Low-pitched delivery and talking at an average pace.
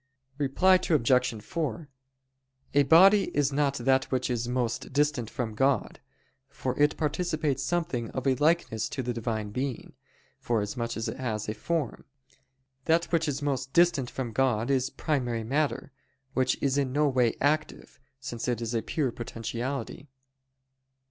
Yes: low, 130 Hz; average, 150 wpm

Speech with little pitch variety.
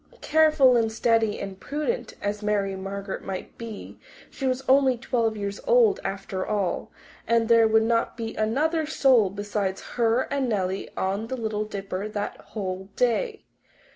No: average, 4.3 semitones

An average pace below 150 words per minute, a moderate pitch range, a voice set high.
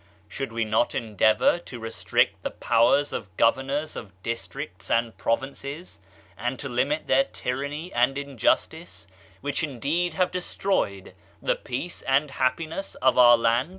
No: average, 140 wpm; average, 4.1 semitones; low, 130 Hz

